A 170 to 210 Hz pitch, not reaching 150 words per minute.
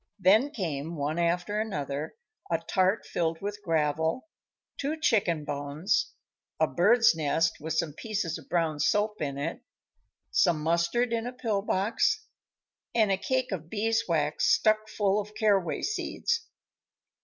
Yes: medium, 185 Hz; average, 140 wpm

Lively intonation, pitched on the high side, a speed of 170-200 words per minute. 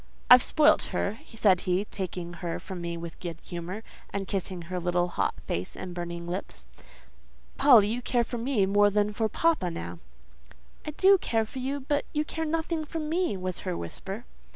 Yes: wide, 6.0 semitones; high, 195 Hz; average, 185 wpm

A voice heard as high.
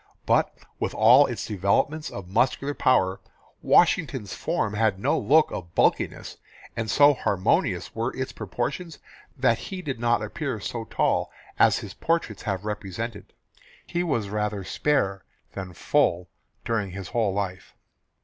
No: low, 105 Hz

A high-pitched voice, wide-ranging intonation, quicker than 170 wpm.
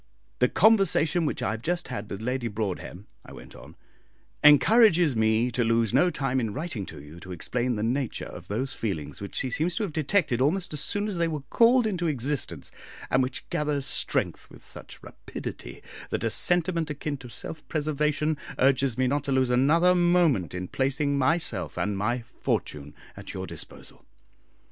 No: low, 135 Hz; wide, 6.1 semitones; average, 180 wpm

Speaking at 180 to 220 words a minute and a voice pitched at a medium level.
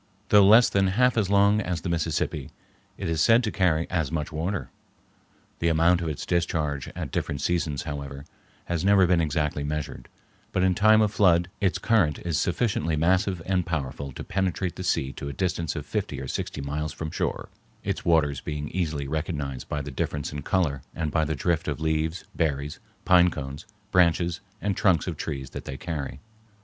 No: average, 190 wpm; very low, 80 Hz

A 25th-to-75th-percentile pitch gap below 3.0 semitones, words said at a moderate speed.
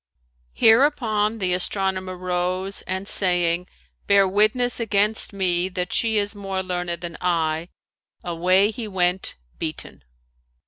No: narrow, 2.6 semitones; slow, 120 wpm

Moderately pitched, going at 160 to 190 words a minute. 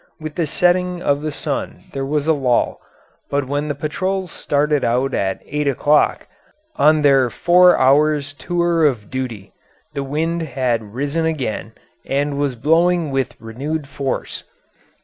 No: medium, 145 Hz; average, 150 wpm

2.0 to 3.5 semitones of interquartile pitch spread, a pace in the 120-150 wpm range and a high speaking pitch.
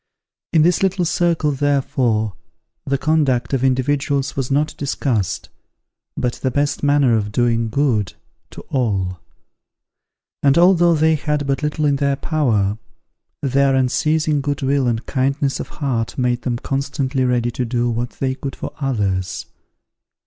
No: average, 3.1 semitones; average, 145 wpm; low, 135 Hz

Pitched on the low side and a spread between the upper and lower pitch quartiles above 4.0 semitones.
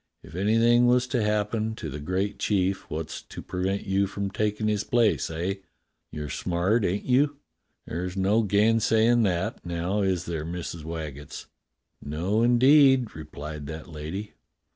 Yes: low, 100 Hz; average, 4.7 semitones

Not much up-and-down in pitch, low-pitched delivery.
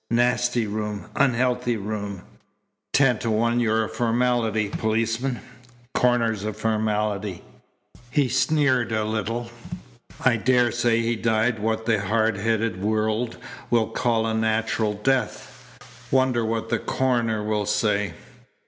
Yes: narrow, 2.0 semitones; low, 115 Hz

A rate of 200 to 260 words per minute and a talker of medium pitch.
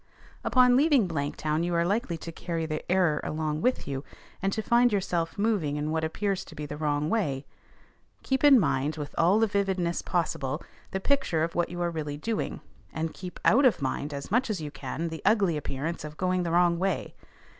Yes: fast, 205 wpm; medium, 170 Hz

